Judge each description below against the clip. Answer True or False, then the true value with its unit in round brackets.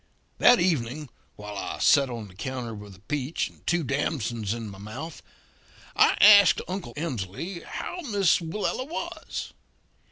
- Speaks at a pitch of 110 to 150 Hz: True (140 Hz)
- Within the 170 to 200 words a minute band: False (150 wpm)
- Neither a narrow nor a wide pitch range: False (7.9 semitones)